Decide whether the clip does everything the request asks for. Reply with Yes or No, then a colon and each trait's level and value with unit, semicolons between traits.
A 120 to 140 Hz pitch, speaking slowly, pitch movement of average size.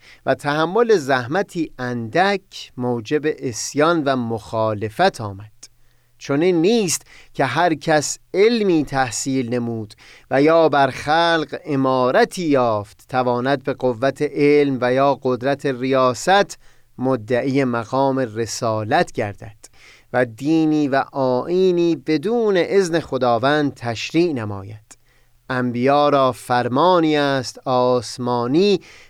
Yes: low, 135 Hz; slow, 100 wpm; average, 4.0 semitones